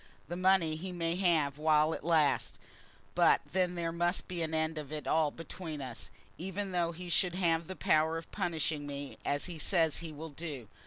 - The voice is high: No, medium, 165 Hz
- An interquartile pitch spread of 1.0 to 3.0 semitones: Yes, narrow, 2.4 semitones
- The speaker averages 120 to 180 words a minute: No, average, 200 wpm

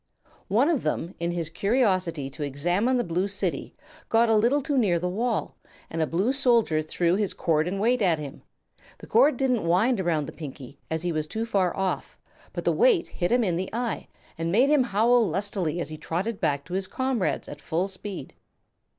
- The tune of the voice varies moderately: No, wide, 5.9 semitones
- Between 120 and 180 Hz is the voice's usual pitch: No, high, 190 Hz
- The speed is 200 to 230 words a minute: Yes, fast, 205 wpm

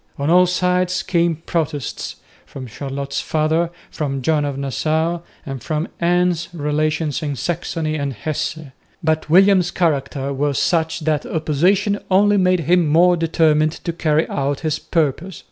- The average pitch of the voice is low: No, medium, 160 Hz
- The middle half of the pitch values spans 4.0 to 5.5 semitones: No, average, 3.0 semitones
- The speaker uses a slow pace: No, average, 145 wpm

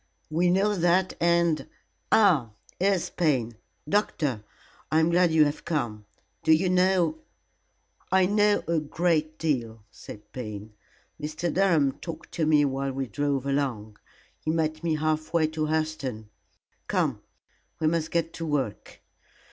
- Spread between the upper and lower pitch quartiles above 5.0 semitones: No, average, 3.9 semitones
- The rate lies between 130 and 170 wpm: Yes, average, 150 wpm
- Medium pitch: Yes, medium, 155 Hz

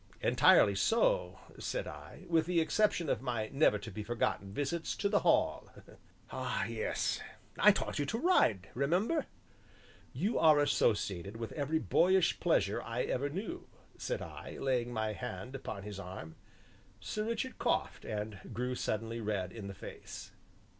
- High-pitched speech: No, low, 130 Hz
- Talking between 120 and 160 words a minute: Yes, average, 155 wpm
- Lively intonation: Yes, wide, 8.9 semitones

